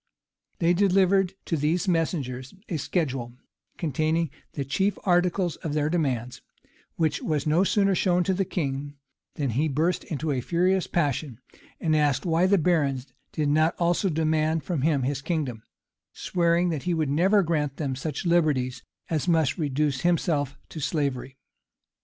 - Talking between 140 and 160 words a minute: Yes, average, 155 wpm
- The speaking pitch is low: No, medium, 155 Hz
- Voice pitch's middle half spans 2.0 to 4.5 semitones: Yes, average, 3.7 semitones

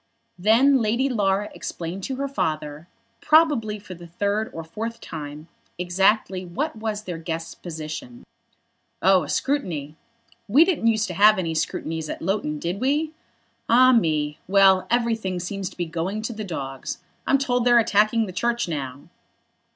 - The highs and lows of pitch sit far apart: Yes, wide, 5.8 semitones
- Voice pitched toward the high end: Yes, high, 195 Hz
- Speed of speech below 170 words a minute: Yes, average, 160 wpm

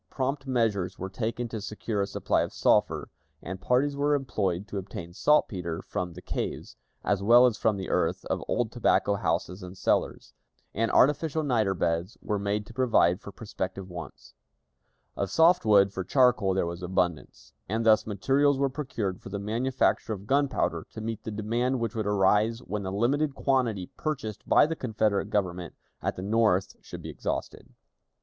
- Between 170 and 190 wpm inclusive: Yes, average, 175 wpm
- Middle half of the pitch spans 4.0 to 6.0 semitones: Yes, average, 4.6 semitones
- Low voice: Yes, low, 105 Hz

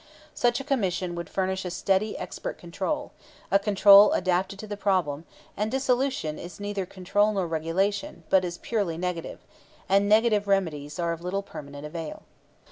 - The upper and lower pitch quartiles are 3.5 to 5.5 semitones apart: No, average, 3.1 semitones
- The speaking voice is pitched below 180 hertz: No, high, 190 Hz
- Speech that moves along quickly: No, average, 160 wpm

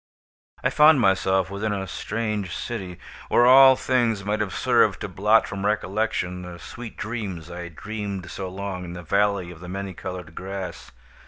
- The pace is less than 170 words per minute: No, average, 175 wpm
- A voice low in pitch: Yes, low, 100 Hz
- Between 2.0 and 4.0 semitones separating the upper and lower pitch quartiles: Yes, average, 3.0 semitones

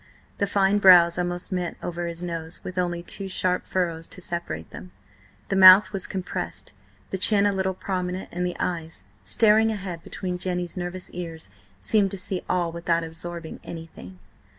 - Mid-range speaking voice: Yes, medium, 180 Hz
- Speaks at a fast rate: No, average, 170 wpm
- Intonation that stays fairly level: Yes, narrow, 1.9 semitones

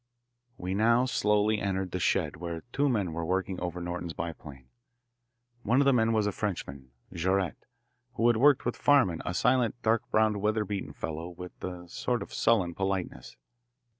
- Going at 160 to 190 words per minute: Yes, average, 165 wpm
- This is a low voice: Yes, very low, 95 Hz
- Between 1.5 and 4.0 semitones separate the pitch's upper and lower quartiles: No, average, 4.4 semitones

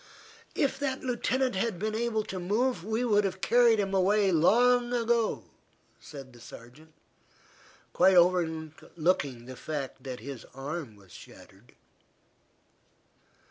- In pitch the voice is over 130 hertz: Yes, medium, 185 Hz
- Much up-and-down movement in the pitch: Yes, wide, 7.8 semitones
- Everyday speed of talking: No, slow, 125 wpm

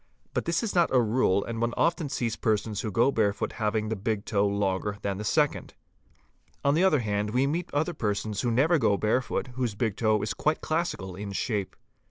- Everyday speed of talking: No, fast, 210 wpm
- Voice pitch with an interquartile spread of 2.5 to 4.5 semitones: No, average, 5.1 semitones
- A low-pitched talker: Yes, low, 110 Hz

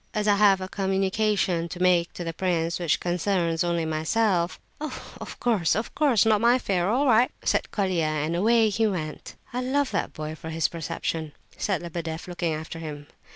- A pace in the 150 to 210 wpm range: Yes, average, 185 wpm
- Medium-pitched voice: Yes, medium, 180 Hz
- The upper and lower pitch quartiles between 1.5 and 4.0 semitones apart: No, average, 4.4 semitones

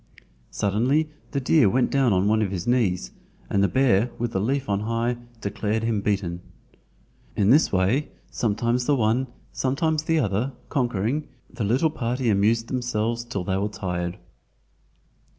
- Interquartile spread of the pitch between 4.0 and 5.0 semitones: Yes, average, 4.3 semitones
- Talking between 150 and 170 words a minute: Yes, average, 155 wpm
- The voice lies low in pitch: Yes, low, 115 Hz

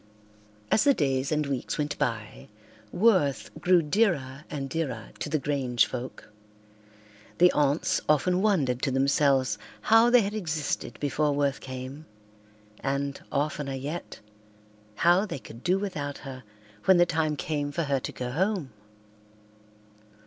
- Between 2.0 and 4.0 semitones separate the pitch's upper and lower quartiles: No, average, 4.4 semitones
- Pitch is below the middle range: No, medium, 145 Hz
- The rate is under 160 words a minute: Yes, average, 140 wpm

